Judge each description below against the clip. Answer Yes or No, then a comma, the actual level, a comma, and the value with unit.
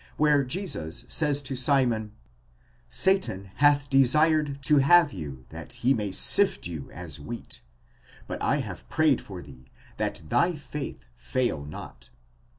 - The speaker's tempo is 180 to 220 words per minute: No, average, 140 wpm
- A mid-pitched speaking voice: No, low, 125 Hz